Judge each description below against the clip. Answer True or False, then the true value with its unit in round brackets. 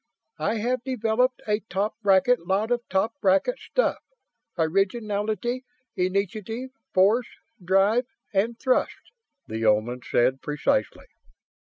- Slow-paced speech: True (110 wpm)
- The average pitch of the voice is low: False (210 Hz)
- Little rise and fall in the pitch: False (4.2 semitones)